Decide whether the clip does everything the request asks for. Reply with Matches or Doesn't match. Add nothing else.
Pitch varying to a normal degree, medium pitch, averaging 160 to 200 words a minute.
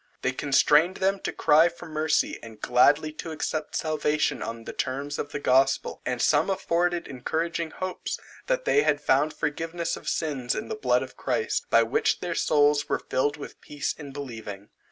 Matches